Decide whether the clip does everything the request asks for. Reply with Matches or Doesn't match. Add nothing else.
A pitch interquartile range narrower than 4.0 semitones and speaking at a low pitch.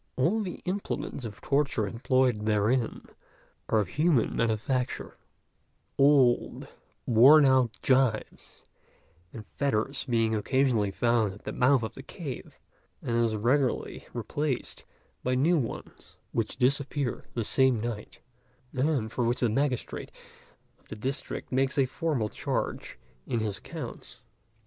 Matches